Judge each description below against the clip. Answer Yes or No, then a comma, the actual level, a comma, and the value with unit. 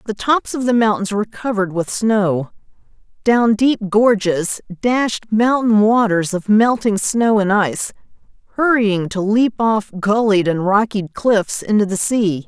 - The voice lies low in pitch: No, high, 210 Hz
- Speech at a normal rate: Yes, average, 150 wpm